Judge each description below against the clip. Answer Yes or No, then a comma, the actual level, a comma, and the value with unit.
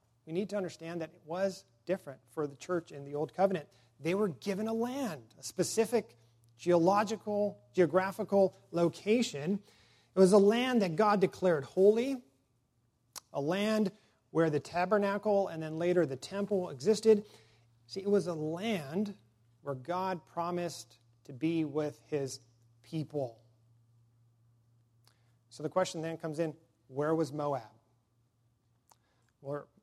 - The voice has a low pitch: No, medium, 160 Hz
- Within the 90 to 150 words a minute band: Yes, slow, 135 wpm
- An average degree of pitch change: No, wide, 8.5 semitones